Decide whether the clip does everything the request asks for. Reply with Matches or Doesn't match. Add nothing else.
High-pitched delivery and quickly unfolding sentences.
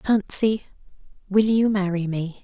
Doesn't match